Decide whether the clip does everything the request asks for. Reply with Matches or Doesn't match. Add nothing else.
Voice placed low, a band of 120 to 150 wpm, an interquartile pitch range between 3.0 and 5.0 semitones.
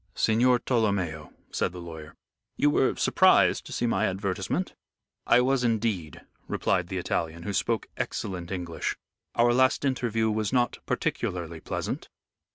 Doesn't match